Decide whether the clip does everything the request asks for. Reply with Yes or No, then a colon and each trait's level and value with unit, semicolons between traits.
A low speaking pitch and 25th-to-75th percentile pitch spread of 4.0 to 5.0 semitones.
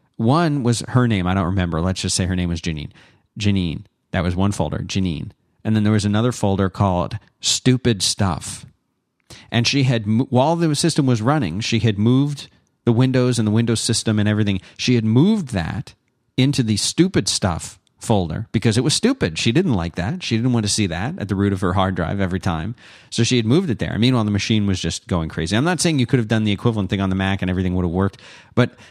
Yes: low, 110 Hz; average, 4.5 semitones